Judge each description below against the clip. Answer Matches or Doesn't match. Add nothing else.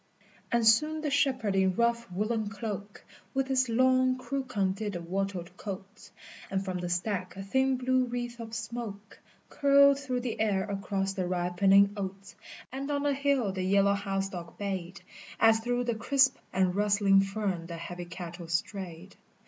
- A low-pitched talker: Doesn't match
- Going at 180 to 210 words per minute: Doesn't match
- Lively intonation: Doesn't match